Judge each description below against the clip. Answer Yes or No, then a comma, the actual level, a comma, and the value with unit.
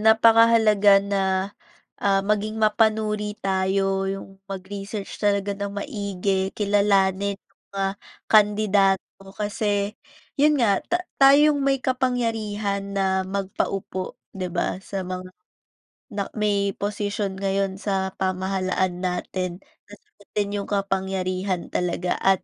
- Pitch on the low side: No, high, 200 Hz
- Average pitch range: No, narrow, 1.6 semitones